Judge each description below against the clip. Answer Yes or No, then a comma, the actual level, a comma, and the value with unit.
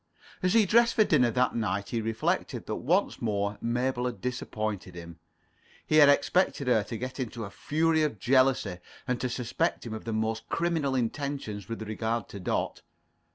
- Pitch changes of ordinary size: Yes, average, 4.2 semitones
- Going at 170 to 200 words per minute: Yes, average, 180 wpm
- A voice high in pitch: No, low, 120 Hz